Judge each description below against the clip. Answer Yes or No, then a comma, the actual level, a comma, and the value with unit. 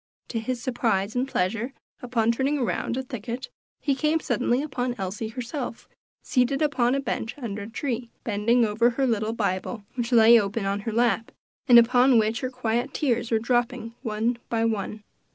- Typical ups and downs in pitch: No, narrow, 2.3 semitones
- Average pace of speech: Yes, average, 175 wpm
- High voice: Yes, high, 235 Hz